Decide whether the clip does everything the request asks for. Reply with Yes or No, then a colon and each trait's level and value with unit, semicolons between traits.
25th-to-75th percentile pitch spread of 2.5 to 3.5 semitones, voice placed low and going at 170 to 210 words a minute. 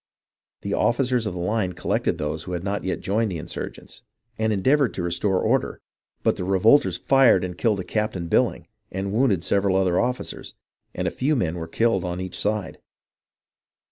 No: average, 4.0 semitones; very low, 95 Hz; average, 180 wpm